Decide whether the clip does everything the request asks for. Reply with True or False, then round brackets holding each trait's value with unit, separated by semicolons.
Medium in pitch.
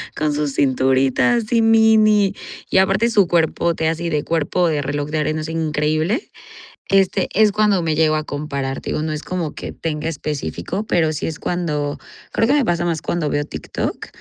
True (160 Hz)